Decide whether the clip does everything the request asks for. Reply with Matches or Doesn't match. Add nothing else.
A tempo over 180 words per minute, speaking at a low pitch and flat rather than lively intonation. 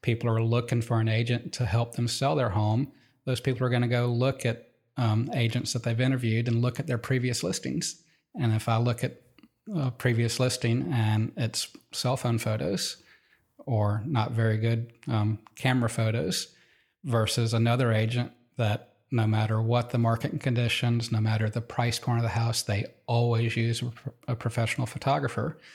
Doesn't match